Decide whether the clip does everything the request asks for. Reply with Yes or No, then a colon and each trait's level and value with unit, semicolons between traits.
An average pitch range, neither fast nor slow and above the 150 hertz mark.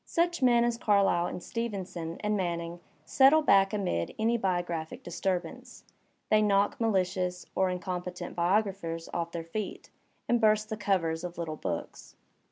Yes: average, 3.7 semitones; average, 150 wpm; high, 190 Hz